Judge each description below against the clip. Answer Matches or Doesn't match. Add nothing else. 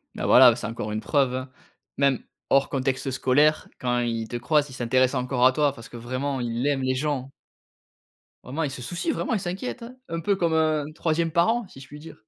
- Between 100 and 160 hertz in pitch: Matches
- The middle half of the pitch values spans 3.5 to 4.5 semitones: Matches